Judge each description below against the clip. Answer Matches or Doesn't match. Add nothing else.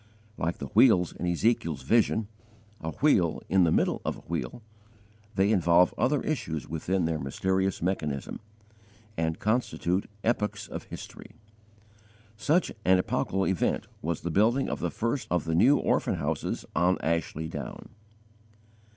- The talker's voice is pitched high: Doesn't match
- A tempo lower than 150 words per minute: Matches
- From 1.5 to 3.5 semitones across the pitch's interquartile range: Doesn't match